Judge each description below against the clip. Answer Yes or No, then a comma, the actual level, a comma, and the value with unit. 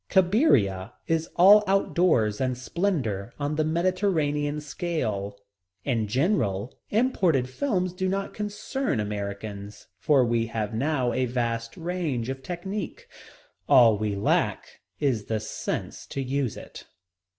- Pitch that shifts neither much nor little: No, wide, 8.1 semitones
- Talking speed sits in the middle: No, slow, 130 wpm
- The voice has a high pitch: No, low, 135 Hz